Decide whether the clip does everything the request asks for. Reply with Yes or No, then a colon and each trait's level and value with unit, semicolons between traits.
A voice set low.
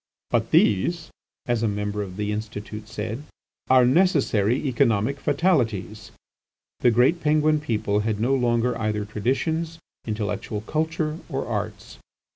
Yes: low, 115 Hz